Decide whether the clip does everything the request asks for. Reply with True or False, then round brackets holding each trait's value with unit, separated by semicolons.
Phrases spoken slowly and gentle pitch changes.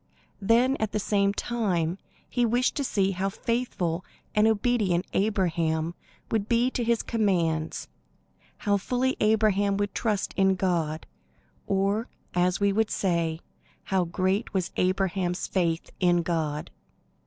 False (130 wpm; 3.8 semitones)